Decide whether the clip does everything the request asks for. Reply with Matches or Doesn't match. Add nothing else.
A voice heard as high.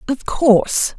Matches